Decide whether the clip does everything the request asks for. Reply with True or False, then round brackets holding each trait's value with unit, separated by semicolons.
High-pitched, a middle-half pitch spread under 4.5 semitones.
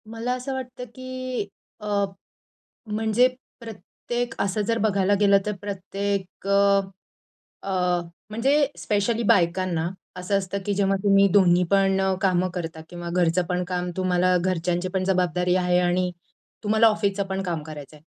True (195 Hz; 2.8 semitones)